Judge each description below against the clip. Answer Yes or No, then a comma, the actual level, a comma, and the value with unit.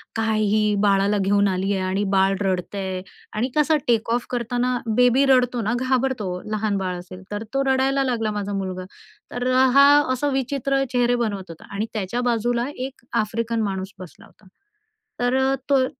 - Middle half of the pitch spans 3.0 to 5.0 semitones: Yes, average, 4.1 semitones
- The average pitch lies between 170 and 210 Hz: No, high, 225 Hz